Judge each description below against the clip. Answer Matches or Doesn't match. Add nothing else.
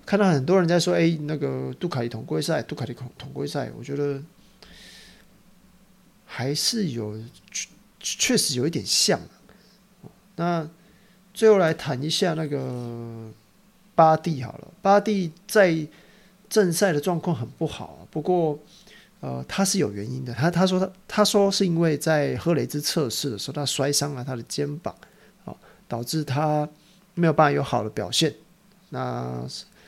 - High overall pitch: Doesn't match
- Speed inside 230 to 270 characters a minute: Doesn't match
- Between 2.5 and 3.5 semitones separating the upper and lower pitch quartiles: Doesn't match